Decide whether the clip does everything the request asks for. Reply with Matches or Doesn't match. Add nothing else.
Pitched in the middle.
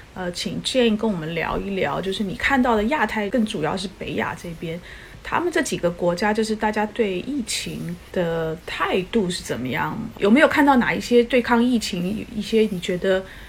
Doesn't match